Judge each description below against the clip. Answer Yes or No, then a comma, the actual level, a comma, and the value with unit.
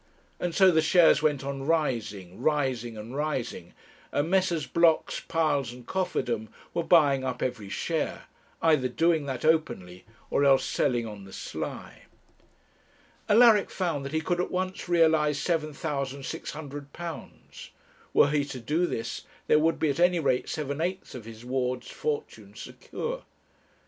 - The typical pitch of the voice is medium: Yes, medium, 150 Hz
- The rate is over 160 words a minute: No, average, 145 wpm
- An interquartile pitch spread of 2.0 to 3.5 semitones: No, average, 4.5 semitones